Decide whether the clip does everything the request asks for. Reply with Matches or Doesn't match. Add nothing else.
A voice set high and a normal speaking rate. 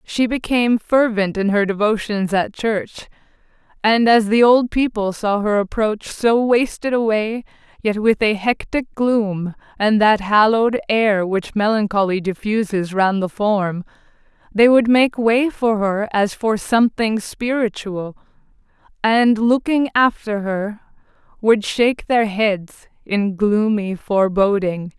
Doesn't match